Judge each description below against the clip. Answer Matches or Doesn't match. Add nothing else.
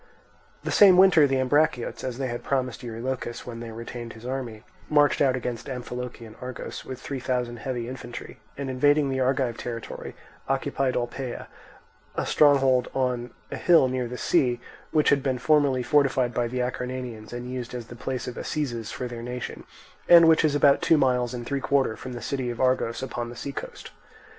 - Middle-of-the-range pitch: Doesn't match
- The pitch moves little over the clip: Matches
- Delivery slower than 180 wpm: Doesn't match